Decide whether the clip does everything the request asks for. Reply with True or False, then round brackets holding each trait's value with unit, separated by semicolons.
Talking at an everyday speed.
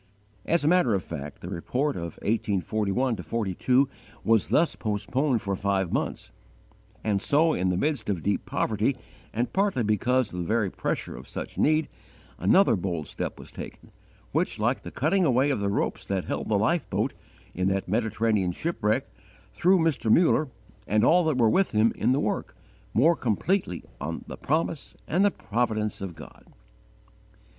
True (170 wpm)